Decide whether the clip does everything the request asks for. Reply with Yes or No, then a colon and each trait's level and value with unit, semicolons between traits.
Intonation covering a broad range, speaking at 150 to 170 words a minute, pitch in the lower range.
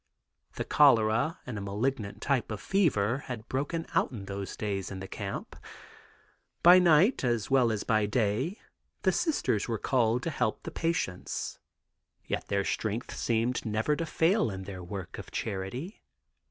Yes: wide, 6.1 semitones; average, 160 wpm; low, 115 Hz